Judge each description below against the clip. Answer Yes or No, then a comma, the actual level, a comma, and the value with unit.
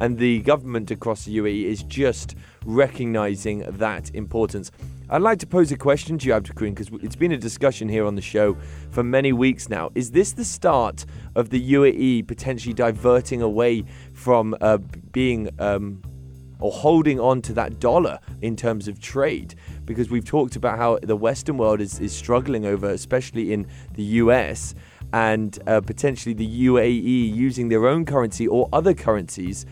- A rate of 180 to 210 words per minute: No, average, 170 wpm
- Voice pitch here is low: Yes, low, 115 Hz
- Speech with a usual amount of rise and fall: Yes, average, 3.4 semitones